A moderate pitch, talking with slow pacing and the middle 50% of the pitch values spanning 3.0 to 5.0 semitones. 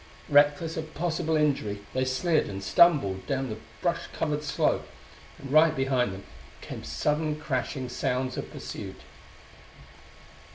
Yes: medium, 145 Hz; slow, 130 wpm; average, 3.6 semitones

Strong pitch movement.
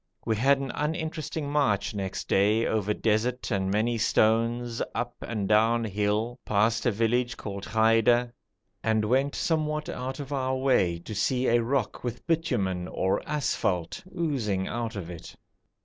No: average, 3.9 semitones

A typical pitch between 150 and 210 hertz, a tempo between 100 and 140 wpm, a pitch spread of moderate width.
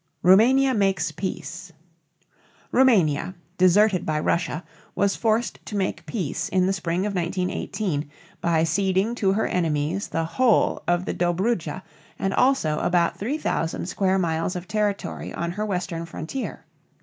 Yes: medium, 185 Hz; slow, 135 wpm; average, 3.6 semitones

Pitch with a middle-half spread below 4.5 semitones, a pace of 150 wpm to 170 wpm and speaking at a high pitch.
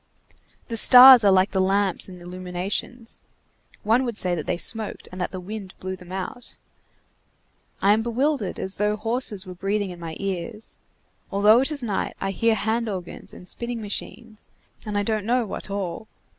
No: average, 3.4 semitones; average, 180 wpm; high, 205 Hz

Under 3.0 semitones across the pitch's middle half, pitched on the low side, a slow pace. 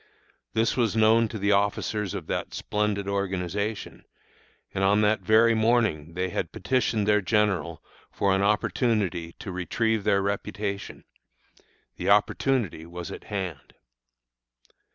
Yes: narrow, 2.4 semitones; low, 100 Hz; slow, 130 wpm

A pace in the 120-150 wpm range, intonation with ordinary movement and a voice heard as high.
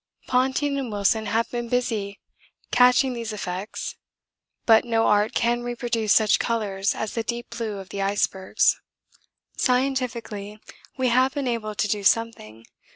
Yes: average, 145 wpm; average, 3.0 semitones; high, 230 Hz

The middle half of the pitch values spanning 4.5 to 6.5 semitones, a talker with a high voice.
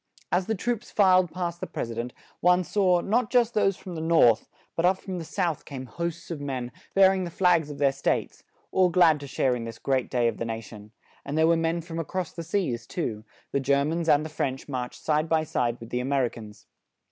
No: wide, 5.6 semitones; medium, 160 Hz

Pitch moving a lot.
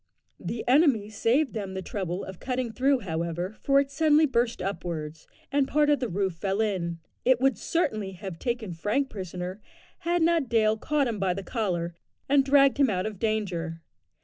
Yes: wide, 6.5 semitones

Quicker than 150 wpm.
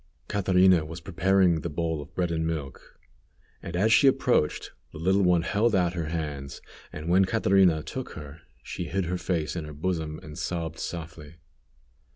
Yes: average, 175 wpm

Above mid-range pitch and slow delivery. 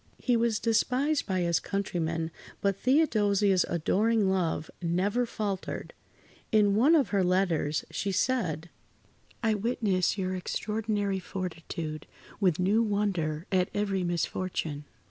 Yes: high, 195 Hz; slow, 120 wpm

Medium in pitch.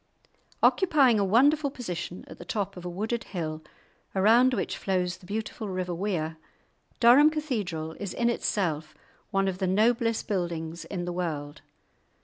No: high, 195 Hz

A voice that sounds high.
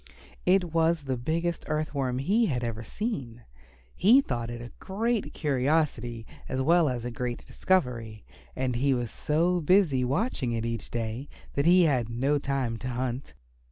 No: low, 135 Hz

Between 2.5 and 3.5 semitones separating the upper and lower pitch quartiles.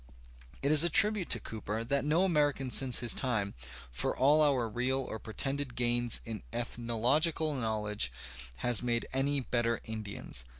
No: average, 4.0 semitones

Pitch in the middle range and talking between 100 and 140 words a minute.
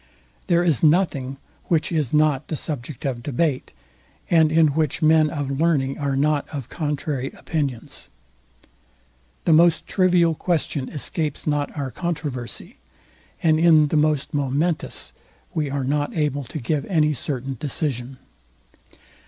Yes: medium, 150 Hz; slow, 135 wpm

